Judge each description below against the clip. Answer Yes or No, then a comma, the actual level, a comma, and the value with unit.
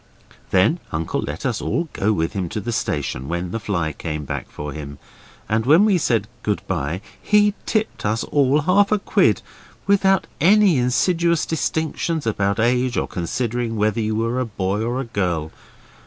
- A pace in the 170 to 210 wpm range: Yes, average, 175 wpm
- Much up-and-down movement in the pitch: Yes, wide, 8.9 semitones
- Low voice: Yes, low, 115 Hz